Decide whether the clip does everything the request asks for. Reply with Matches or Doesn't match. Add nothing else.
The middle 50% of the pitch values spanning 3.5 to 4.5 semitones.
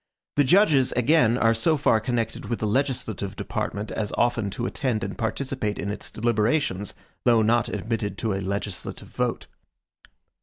Doesn't match